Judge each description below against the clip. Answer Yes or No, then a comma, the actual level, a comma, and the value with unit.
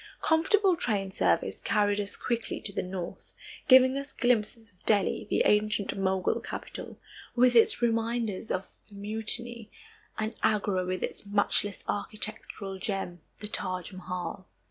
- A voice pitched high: Yes, high, 210 Hz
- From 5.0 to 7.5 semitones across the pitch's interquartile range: No, average, 3.3 semitones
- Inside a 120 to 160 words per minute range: Yes, average, 140 wpm